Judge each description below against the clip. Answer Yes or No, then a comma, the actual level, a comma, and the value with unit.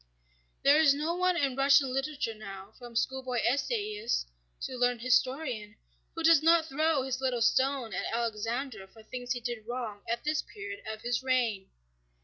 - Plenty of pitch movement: No, average, 3.8 semitones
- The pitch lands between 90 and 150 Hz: No, very high, 255 Hz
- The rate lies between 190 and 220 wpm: No, average, 165 wpm